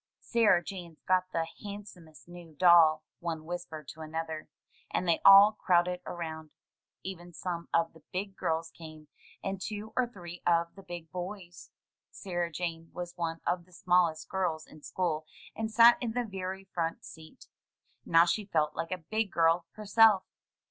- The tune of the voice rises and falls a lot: No, average, 2.7 semitones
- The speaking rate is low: No, average, 160 wpm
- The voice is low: No, medium, 175 Hz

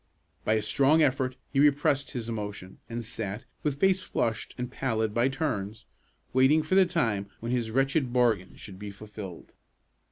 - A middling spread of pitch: Yes, average, 4.5 semitones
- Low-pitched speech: Yes, low, 120 Hz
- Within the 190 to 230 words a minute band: No, average, 165 wpm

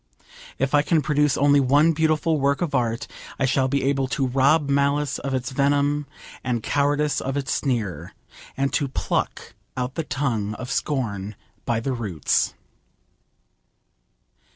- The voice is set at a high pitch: No, medium, 140 Hz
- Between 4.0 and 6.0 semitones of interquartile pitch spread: No, narrow, 2.5 semitones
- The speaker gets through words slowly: No, average, 150 wpm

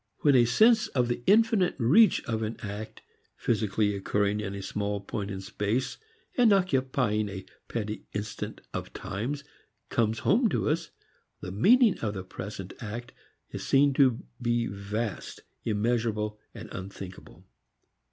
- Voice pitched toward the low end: Yes, low, 110 Hz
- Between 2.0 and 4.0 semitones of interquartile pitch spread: No, average, 4.4 semitones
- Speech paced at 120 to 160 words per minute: Yes, average, 140 wpm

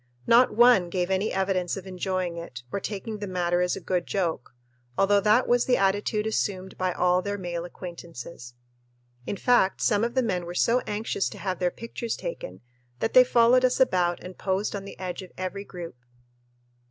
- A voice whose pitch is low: No, high, 190 Hz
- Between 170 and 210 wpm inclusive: Yes, average, 190 wpm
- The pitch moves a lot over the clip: No, average, 3.4 semitones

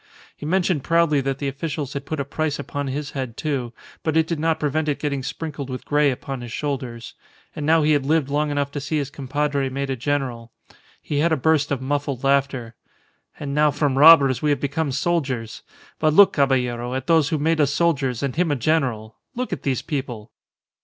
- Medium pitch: Yes, medium, 145 Hz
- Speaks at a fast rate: Yes, fast, 210 wpm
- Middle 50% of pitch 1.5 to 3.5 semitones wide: Yes, narrow, 2.5 semitones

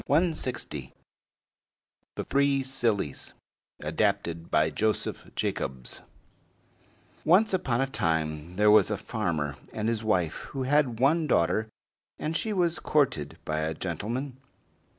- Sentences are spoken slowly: Yes, slow, 115 wpm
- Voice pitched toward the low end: Yes, low, 110 Hz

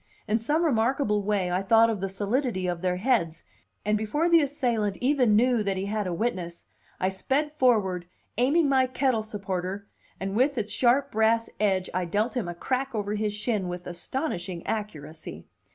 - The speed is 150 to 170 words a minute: No, average, 180 wpm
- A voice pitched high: Yes, high, 210 Hz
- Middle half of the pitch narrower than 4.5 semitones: No, average, 5.1 semitones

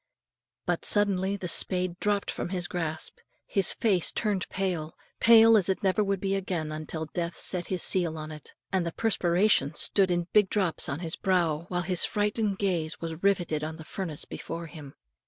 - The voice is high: No, medium, 180 Hz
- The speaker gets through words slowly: No, average, 185 wpm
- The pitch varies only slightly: No, average, 3.2 semitones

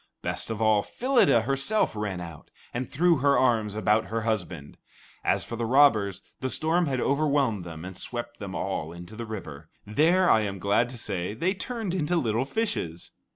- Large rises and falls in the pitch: Yes, wide, 6.1 semitones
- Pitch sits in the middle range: No, low, 115 Hz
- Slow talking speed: No, average, 185 wpm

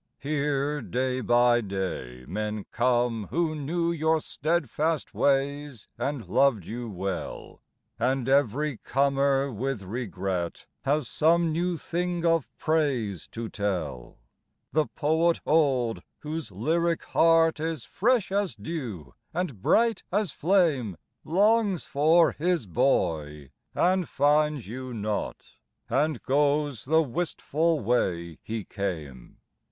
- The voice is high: No, medium, 140 Hz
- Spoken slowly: Yes, slow, 115 wpm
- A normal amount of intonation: No, wide, 6.4 semitones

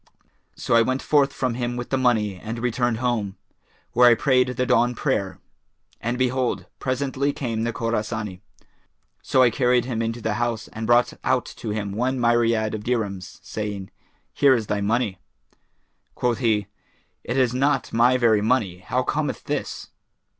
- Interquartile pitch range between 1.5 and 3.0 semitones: Yes, narrow, 2.5 semitones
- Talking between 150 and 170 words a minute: Yes, average, 165 wpm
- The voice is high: No, low, 120 Hz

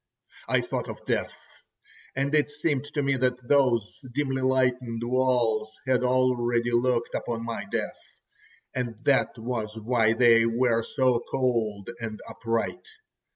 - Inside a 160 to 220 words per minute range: No, slow, 135 wpm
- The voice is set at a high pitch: No, low, 120 Hz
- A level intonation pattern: Yes, narrow, 2.0 semitones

